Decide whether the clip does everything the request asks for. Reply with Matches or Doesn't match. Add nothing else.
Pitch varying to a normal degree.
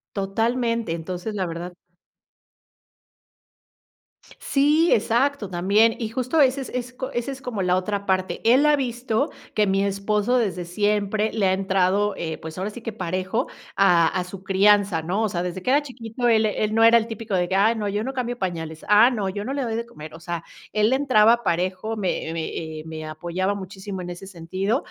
Matches